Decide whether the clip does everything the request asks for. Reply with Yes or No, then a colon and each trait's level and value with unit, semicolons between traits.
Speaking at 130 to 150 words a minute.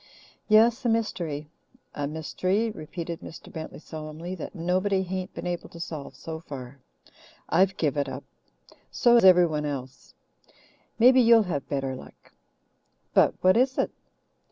Yes: average, 145 wpm